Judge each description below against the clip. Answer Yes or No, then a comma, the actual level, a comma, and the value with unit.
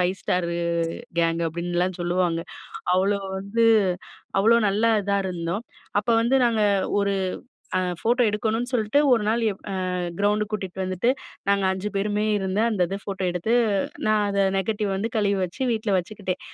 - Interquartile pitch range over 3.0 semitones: No, average, 2.7 semitones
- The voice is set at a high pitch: Yes, high, 200 Hz